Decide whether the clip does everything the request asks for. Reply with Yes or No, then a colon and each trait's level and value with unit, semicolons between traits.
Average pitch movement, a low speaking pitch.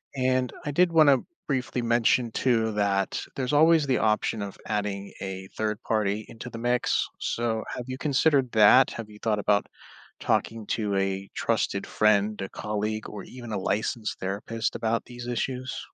Yes: average, 3.4 semitones; low, 115 Hz